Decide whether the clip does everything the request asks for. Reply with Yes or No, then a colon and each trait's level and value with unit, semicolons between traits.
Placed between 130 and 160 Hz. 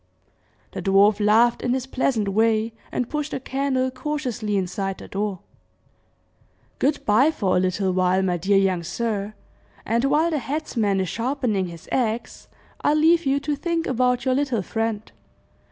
No: high, 230 Hz